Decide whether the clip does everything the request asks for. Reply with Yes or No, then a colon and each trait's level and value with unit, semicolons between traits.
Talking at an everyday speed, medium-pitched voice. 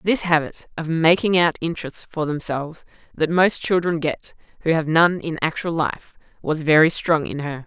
Yes: average, 180 wpm; medium, 160 Hz